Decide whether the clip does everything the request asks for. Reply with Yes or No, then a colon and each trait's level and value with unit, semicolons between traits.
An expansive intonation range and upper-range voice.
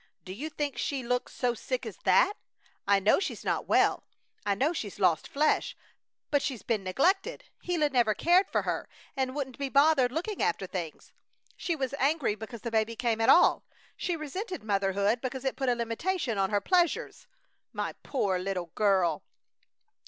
Yes: wide, 6.7 semitones; very high, 250 Hz